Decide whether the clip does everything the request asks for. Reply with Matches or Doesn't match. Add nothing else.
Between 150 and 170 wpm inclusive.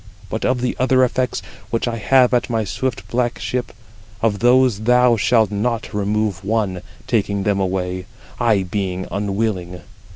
Matches